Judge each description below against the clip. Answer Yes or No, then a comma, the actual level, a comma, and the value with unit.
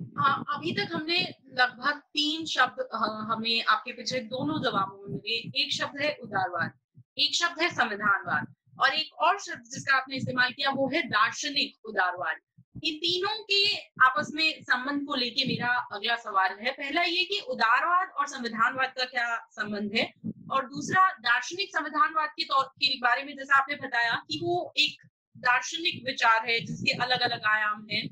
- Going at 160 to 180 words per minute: Yes, average, 165 wpm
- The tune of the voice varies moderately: Yes, average, 4.9 semitones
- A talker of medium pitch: No, very high, 265 Hz